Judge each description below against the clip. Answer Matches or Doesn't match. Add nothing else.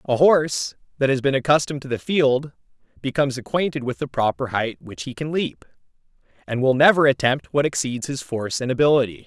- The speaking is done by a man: Matches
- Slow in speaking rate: Doesn't match